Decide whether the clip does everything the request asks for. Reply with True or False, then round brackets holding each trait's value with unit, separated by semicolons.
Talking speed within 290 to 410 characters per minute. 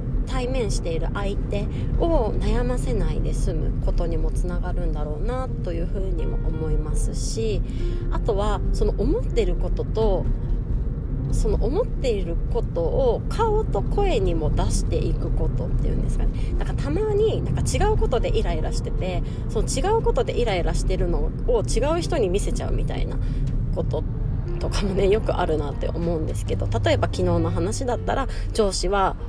True (350 characters per minute)